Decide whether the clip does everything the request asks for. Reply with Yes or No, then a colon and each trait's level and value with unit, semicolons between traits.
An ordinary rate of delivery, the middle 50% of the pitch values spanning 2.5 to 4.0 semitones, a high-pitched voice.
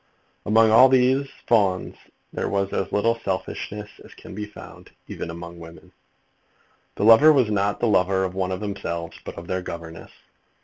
No: average, 170 wpm; average, 3.4 semitones; low, 100 Hz